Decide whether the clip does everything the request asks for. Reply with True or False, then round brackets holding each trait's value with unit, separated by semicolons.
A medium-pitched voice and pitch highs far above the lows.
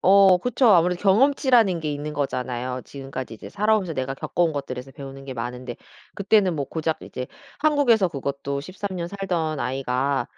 True (155 Hz; 6.3 semitones)